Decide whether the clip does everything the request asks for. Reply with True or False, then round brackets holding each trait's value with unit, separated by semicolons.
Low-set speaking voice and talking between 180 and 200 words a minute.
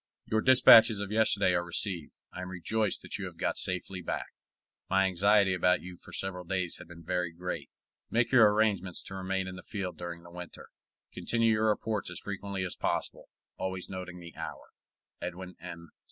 True (95 Hz; 185 wpm)